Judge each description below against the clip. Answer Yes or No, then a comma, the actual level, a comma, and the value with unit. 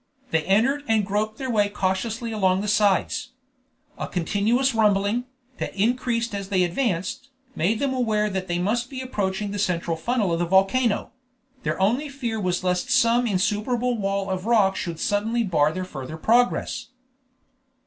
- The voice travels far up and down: No, average, 4.0 semitones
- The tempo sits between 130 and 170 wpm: Yes, average, 160 wpm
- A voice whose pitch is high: Yes, high, 205 Hz